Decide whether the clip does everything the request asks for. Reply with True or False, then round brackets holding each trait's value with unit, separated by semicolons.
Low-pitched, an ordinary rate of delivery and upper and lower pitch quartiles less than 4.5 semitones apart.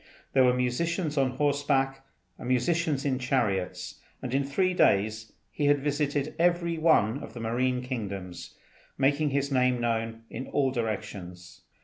True (130 Hz; 145 wpm; 4.0 semitones)